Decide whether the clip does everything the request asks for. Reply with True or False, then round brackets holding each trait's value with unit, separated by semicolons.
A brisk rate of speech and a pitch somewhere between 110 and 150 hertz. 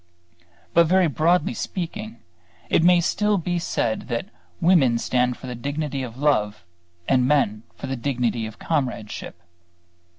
False (140 wpm; 140 Hz)